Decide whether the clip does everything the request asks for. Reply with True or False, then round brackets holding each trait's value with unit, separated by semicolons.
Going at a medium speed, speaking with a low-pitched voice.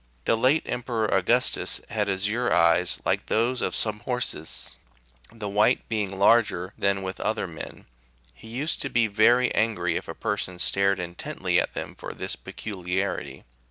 True (160 wpm; 105 Hz)